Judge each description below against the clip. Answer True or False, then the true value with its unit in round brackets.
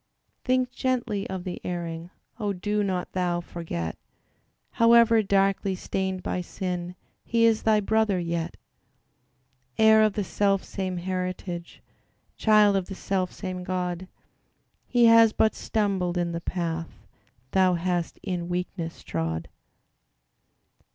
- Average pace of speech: False (120 wpm)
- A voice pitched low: False (185 Hz)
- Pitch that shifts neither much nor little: True (3.1 semitones)